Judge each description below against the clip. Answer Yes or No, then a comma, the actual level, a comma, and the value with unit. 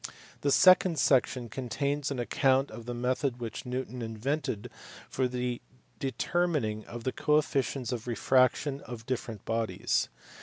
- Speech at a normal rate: No, slow, 130 wpm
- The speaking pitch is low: Yes, low, 125 Hz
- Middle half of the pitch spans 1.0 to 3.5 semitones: Yes, average, 2.8 semitones